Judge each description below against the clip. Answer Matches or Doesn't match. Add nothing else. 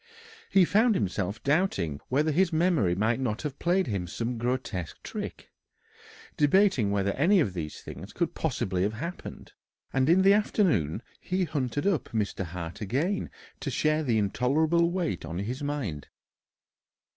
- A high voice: Doesn't match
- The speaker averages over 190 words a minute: Doesn't match